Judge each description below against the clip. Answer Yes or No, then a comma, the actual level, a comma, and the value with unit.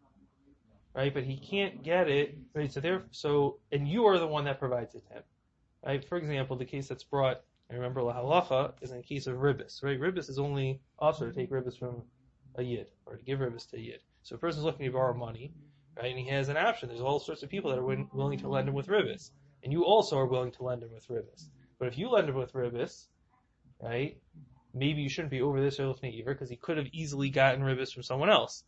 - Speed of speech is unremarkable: No, fast, 250 wpm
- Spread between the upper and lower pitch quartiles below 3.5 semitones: Yes, narrow, 2.5 semitones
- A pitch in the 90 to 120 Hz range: No, low, 135 Hz